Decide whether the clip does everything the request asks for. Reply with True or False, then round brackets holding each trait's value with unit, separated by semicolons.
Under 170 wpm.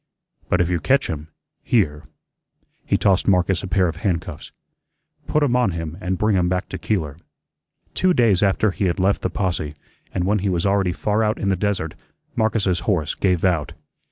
False (190 wpm)